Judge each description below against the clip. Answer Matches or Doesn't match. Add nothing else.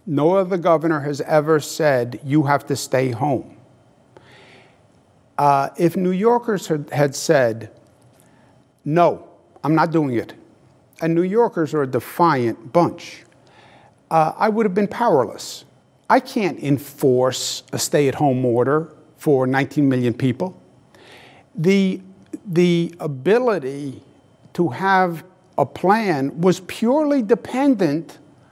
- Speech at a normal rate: Doesn't match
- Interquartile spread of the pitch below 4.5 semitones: Doesn't match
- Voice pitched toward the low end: Doesn't match